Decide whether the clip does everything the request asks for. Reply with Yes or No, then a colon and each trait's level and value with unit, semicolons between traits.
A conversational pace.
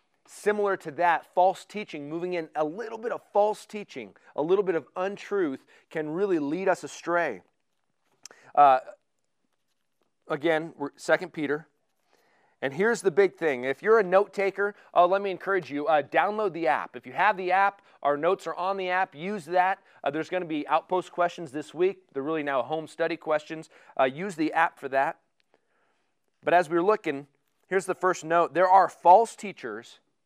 Yes: average, 180 wpm